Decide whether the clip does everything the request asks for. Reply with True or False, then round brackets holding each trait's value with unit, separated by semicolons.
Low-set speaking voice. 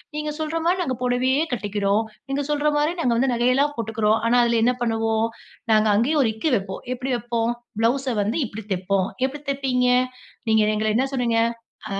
False (240 Hz)